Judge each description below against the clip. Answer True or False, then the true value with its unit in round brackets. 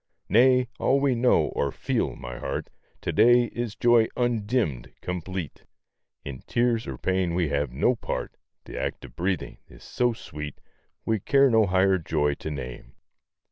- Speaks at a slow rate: False (160 wpm)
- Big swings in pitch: True (8.3 semitones)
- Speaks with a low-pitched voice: True (95 Hz)